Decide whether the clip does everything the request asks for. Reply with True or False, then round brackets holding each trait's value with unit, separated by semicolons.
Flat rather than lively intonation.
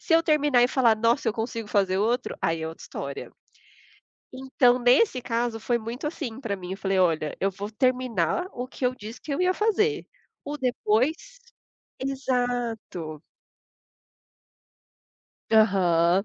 False (4.7 semitones)